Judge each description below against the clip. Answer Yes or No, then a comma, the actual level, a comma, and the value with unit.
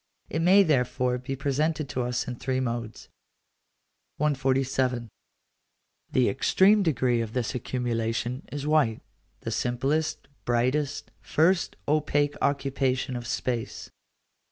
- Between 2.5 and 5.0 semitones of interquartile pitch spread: Yes, average, 3.2 semitones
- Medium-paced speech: No, slow, 110 wpm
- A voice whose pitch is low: Yes, low, 130 Hz